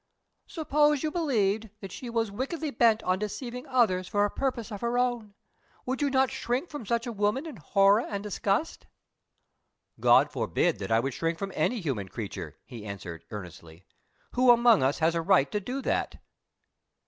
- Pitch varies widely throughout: Yes, wide, 6.2 semitones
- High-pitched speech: Yes, high, 215 Hz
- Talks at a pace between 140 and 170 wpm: No, average, 180 wpm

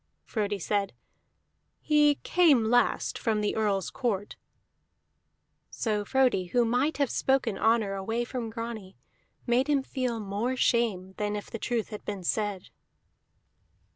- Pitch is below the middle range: No, high, 225 Hz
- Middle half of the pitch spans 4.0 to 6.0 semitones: No, average, 3.3 semitones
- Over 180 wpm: No, slow, 135 wpm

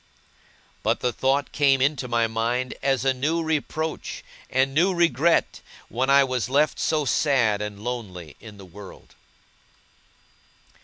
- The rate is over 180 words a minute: No, average, 140 wpm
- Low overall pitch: Yes, low, 130 Hz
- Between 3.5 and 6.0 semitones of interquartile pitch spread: Yes, average, 3.8 semitones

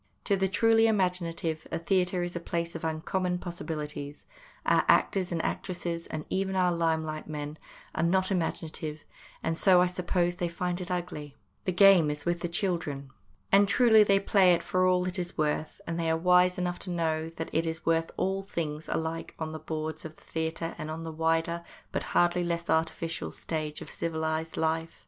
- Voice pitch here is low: No, medium, 170 Hz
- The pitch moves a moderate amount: No, narrow, 2.1 semitones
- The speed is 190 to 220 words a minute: Yes, average, 195 wpm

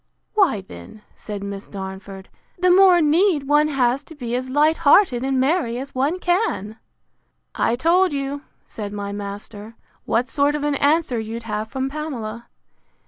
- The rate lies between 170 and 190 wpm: No, average, 160 wpm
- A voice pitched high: Yes, very high, 265 Hz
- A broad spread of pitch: Yes, wide, 6.0 semitones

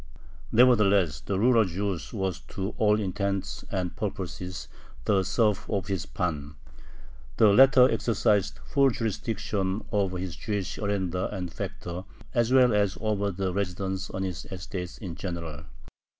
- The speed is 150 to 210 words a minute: No, slow, 135 wpm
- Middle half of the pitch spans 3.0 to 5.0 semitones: No, narrow, 2.5 semitones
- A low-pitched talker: Yes, very low, 95 Hz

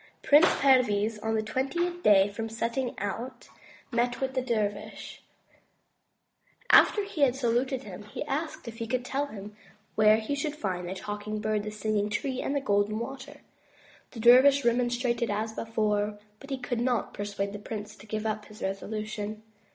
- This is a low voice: No, high, 225 Hz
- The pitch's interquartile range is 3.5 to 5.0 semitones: Yes, average, 3.8 semitones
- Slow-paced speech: No, average, 175 wpm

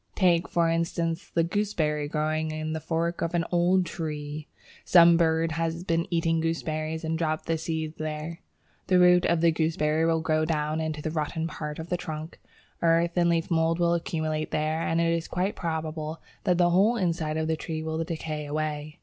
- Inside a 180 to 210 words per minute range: Yes, average, 190 wpm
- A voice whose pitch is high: No, medium, 160 Hz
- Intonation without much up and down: Yes, narrow, 1.3 semitones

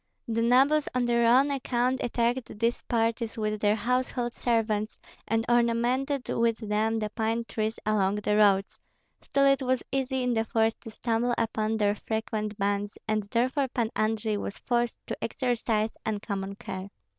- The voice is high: Yes, high, 225 Hz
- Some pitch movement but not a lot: No, narrow, 2.3 semitones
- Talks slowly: No, average, 160 wpm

